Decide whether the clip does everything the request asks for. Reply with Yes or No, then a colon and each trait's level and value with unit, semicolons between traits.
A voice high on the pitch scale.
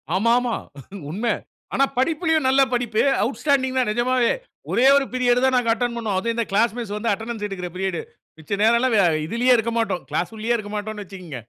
Yes: high, 230 Hz